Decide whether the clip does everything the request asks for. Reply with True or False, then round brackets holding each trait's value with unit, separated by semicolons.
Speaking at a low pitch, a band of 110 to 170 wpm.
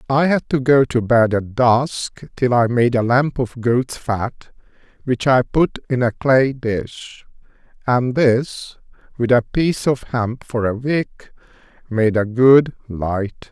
True (125 Hz; 165 wpm)